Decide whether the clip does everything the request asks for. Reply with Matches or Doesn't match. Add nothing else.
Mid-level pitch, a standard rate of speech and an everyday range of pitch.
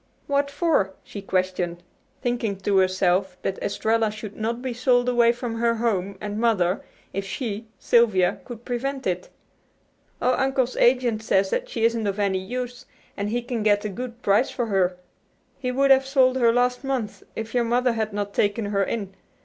Doesn't match